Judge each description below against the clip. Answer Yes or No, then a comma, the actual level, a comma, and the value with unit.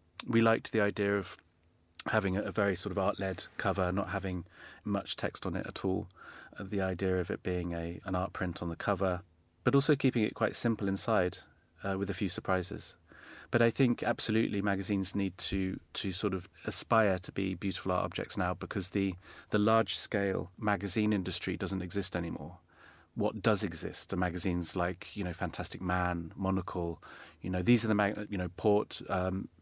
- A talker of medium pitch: No, very low, 95 Hz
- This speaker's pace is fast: No, average, 185 wpm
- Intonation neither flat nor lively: No, narrow, 2.2 semitones